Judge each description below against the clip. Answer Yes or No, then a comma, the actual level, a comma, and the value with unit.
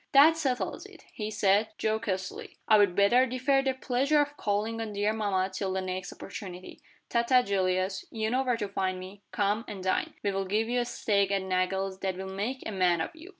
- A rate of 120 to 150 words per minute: No, fast, 205 wpm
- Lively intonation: No, average, 4.1 semitones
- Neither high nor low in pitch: No, high, 205 Hz